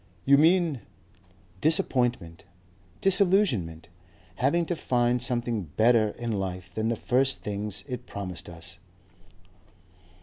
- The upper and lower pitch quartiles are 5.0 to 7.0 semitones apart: Yes, wide, 5.6 semitones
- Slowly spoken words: Yes, slow, 105 wpm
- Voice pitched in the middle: No, low, 120 Hz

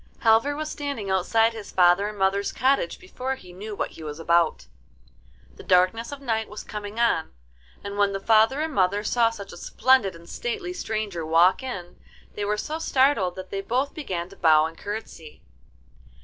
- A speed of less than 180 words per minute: No, average, 185 wpm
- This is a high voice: Yes, high, 205 Hz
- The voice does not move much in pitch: No, average, 5.2 semitones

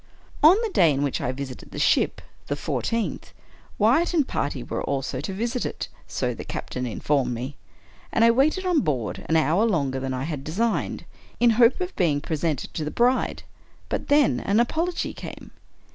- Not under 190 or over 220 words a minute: Yes, average, 195 wpm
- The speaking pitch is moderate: Yes, medium, 165 Hz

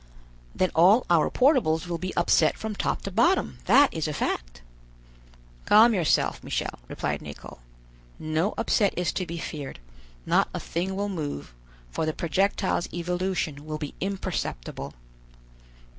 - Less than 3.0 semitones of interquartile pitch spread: No, average, 4.0 semitones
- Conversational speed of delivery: Yes, average, 145 wpm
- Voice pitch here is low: No, medium, 175 Hz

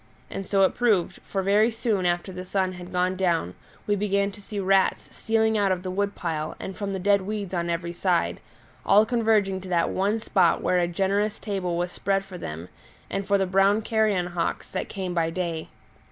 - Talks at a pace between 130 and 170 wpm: No, fast, 205 wpm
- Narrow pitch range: Yes, narrow, 2.3 semitones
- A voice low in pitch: No, high, 190 Hz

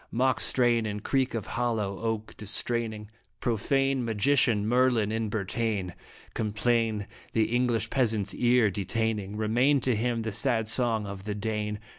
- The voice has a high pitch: No, low, 110 Hz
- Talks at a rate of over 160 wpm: No, average, 140 wpm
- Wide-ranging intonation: No, narrow, 2.4 semitones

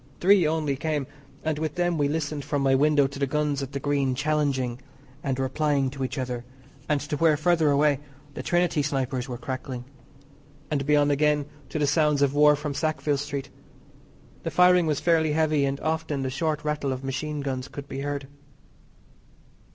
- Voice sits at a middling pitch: Yes, medium, 145 Hz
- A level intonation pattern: Yes, narrow, 1.9 semitones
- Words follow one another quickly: No, average, 180 wpm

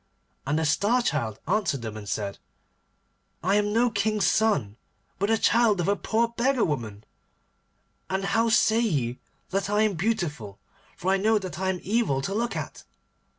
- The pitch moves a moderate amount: No, wide, 7.1 semitones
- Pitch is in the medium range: No, high, 195 Hz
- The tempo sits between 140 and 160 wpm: No, average, 175 wpm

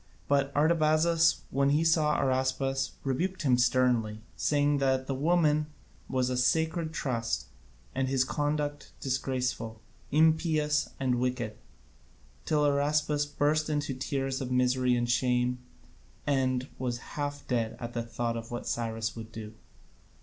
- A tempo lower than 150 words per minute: Yes, slow, 135 wpm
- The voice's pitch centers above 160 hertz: No, low, 135 Hz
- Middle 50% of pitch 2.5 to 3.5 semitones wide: Yes, average, 3.1 semitones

